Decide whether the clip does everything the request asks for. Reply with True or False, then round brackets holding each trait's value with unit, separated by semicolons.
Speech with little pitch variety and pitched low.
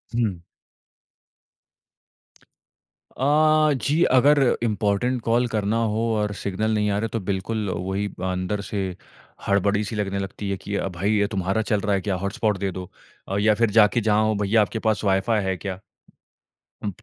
True (2.3 semitones; 105 Hz)